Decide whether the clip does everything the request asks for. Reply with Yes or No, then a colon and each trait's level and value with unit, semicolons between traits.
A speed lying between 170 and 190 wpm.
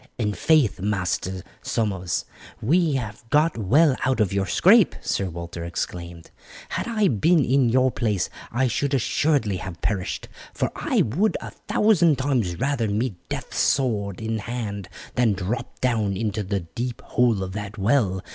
No: average, 155 wpm